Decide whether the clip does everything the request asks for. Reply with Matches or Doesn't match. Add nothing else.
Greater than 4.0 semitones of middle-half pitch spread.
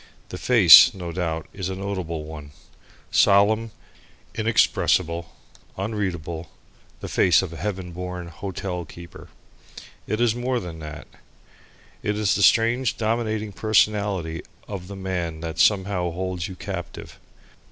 Doesn't match